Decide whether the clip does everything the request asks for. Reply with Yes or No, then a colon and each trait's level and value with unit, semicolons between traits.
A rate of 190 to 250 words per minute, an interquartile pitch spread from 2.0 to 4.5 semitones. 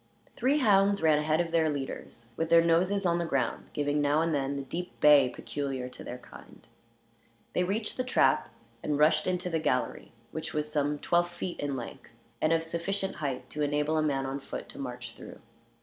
Yes: average, 200 wpm; average, 3.5 semitones